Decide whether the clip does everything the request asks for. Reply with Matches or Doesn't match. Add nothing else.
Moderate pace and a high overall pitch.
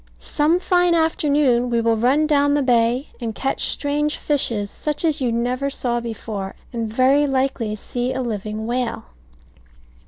Matches